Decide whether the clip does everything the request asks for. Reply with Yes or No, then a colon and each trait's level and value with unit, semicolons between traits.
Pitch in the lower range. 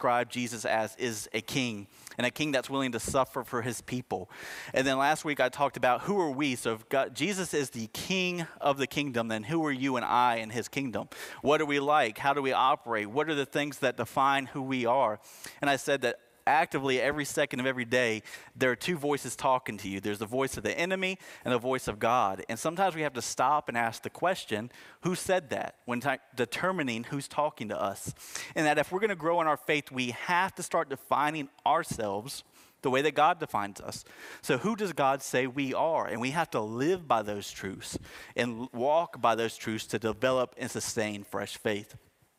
Yes: low, 130 Hz